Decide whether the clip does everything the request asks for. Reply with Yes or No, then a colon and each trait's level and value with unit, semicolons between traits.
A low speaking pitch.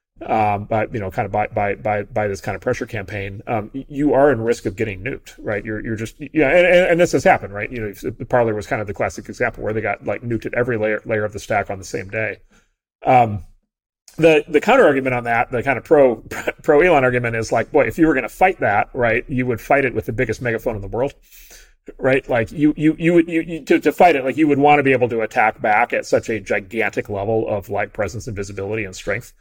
Yes: low, 115 Hz